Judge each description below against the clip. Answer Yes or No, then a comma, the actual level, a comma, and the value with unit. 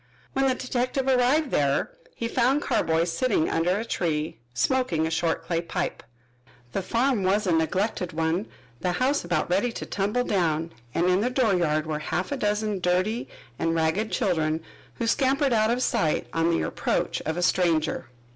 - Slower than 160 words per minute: No, average, 175 wpm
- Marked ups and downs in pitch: Yes, wide, 6.7 semitones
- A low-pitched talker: No, medium, 185 Hz